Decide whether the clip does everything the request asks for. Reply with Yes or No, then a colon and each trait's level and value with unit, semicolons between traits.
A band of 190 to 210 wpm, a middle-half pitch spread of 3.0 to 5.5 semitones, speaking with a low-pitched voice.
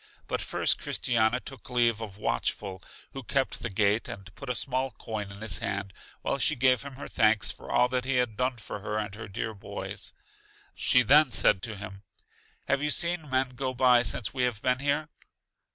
Yes: average, 200 wpm; average, 3.6 semitones; low, 125 Hz